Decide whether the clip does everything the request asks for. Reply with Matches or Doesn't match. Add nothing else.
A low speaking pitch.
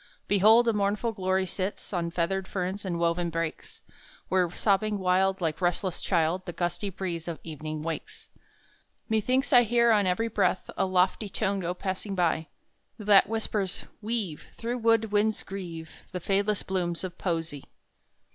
Doesn't match